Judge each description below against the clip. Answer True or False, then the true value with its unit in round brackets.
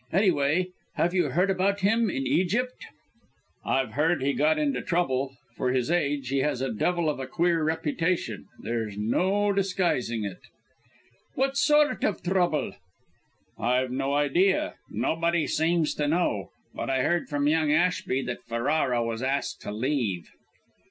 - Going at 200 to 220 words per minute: False (150 wpm)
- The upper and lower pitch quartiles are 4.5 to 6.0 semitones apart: True (5.3 semitones)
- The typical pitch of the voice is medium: True (150 Hz)